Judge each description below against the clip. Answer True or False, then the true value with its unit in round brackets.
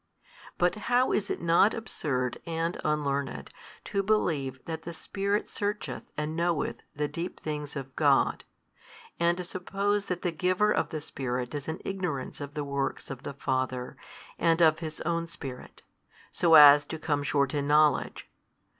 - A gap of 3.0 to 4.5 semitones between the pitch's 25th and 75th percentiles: True (3.9 semitones)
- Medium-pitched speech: True (155 Hz)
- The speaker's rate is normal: True (165 wpm)